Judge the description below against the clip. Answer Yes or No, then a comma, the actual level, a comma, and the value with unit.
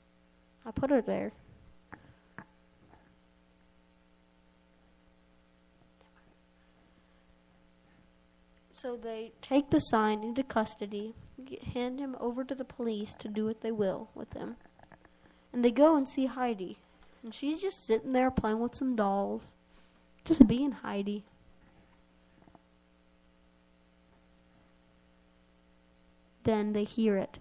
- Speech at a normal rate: No, slow, 100 wpm